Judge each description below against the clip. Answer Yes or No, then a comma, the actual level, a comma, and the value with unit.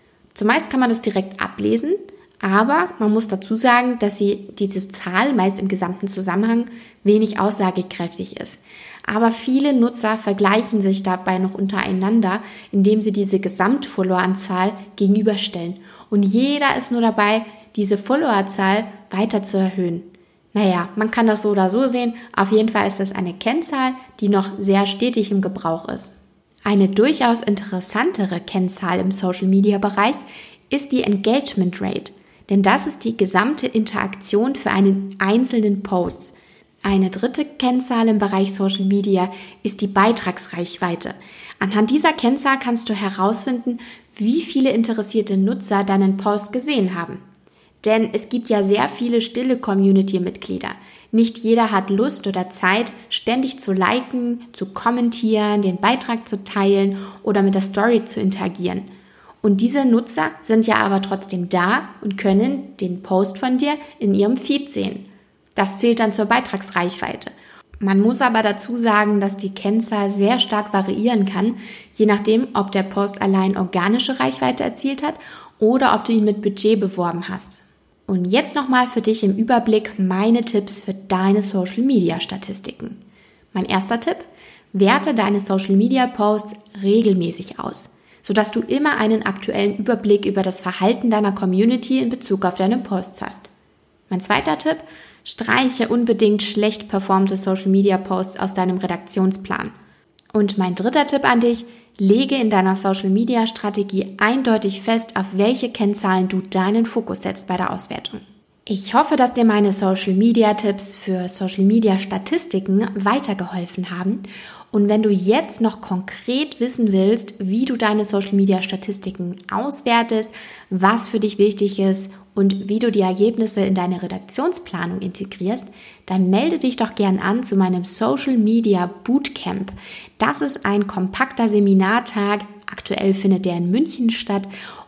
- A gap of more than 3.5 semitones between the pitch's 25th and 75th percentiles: No, average, 3.1 semitones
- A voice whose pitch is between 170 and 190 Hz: No, high, 205 Hz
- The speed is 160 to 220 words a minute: No, average, 140 wpm